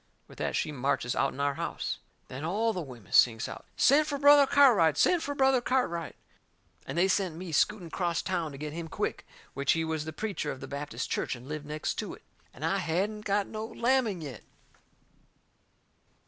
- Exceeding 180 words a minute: Yes, average, 195 wpm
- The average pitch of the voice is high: No, medium, 170 Hz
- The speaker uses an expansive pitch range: Yes, wide, 6.8 semitones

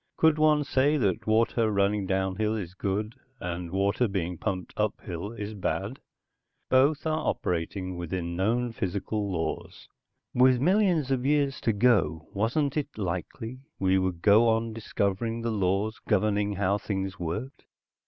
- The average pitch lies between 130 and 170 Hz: No, low, 105 Hz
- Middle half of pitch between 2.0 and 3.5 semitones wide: No, average, 4.5 semitones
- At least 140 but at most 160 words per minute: Yes, average, 150 wpm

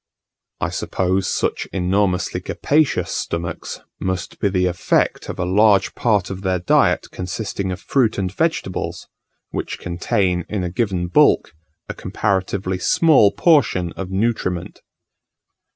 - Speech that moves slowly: Yes, slow, 130 wpm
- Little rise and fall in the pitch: Yes, narrow, 2.3 semitones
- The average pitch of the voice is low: Yes, very low, 95 Hz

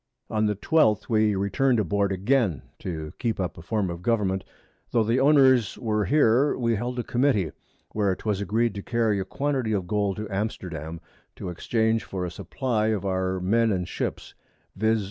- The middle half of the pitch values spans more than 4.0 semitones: No, average, 3.5 semitones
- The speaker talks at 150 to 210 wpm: Yes, average, 185 wpm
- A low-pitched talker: Yes, low, 105 Hz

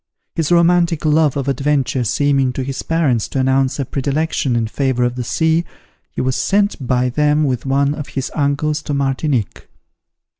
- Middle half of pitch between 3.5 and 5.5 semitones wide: No, average, 2.7 semitones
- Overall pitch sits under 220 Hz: Yes, medium, 140 Hz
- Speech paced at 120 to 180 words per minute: Yes, average, 175 wpm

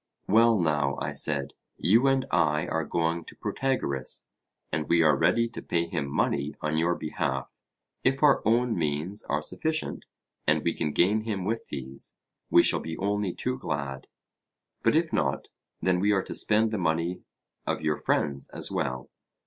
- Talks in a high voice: No, very low, 85 Hz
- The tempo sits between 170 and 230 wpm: Yes, average, 175 wpm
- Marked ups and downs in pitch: Yes, wide, 6.5 semitones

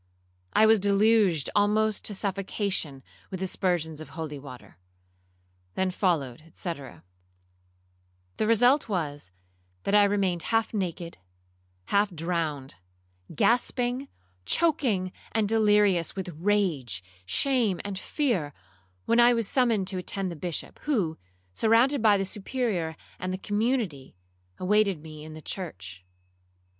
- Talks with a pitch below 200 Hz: Yes, medium, 185 Hz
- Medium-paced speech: No, slow, 120 wpm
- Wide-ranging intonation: Yes, wide, 5.7 semitones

